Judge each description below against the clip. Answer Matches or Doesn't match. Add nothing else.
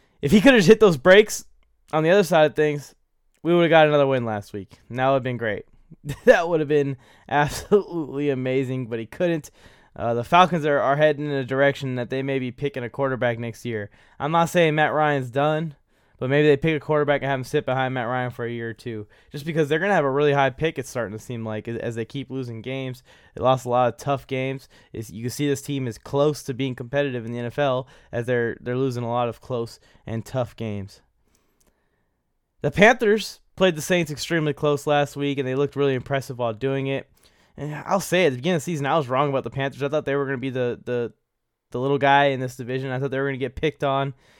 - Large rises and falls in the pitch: Doesn't match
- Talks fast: Matches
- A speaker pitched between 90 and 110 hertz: Doesn't match